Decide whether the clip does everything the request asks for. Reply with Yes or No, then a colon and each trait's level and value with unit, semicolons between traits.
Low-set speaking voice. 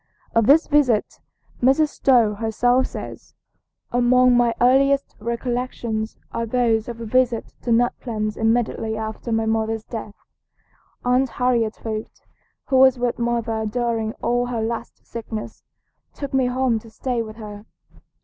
No: high, 235 Hz